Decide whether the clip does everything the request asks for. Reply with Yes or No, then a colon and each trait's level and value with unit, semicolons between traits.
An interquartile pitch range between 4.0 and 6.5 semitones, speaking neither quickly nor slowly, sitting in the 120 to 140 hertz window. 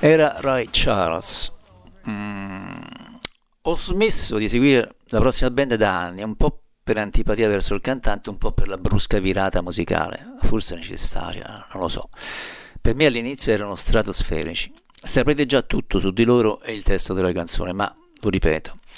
No: average, 4.8 semitones; average, 160 wpm; low, 110 Hz